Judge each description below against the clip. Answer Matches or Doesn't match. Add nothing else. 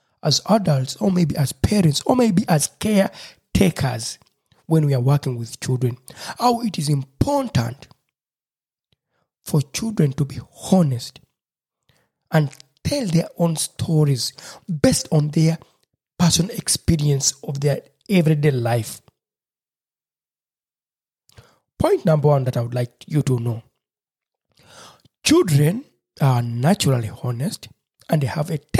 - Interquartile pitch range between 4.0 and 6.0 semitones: Matches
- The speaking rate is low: Matches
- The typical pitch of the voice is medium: Matches